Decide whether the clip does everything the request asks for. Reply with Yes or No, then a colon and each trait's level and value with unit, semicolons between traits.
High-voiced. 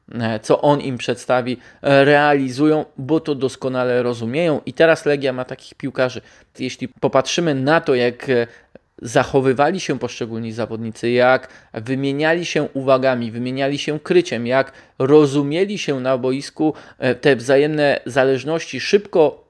No: low, 135 Hz